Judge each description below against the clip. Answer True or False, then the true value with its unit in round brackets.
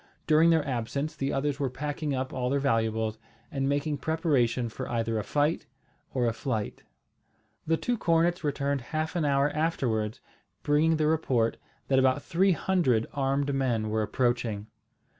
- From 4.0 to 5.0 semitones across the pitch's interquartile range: True (4.4 semitones)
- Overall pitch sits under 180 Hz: True (140 Hz)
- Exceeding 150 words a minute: True (160 wpm)